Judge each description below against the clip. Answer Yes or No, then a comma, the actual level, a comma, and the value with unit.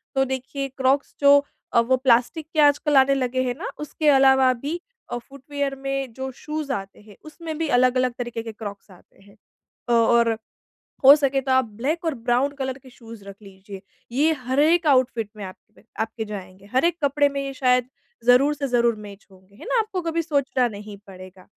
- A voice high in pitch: Yes, very high, 260 Hz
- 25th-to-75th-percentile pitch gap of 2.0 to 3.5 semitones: No, average, 3.9 semitones